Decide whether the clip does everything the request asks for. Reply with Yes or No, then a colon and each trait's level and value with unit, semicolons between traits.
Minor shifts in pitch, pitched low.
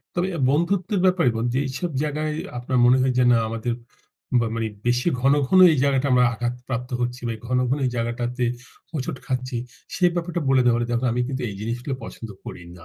No: average, 3.4 semitones; low, 125 Hz